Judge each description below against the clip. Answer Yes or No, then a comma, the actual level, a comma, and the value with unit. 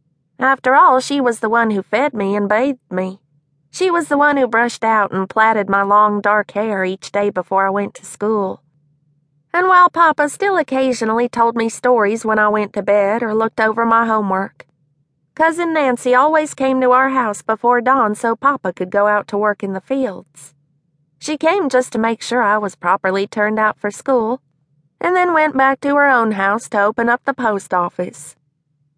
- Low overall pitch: No, high, 215 Hz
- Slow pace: No, average, 200 wpm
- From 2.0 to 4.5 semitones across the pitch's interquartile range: No, average, 5.2 semitones